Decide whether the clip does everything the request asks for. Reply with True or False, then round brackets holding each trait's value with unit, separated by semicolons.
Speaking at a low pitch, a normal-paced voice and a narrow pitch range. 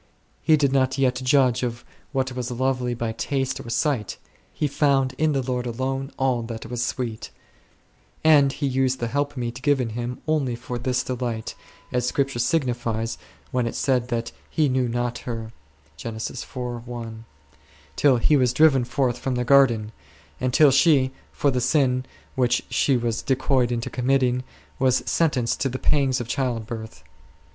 True (125 Hz; 155 wpm; 2.1 semitones)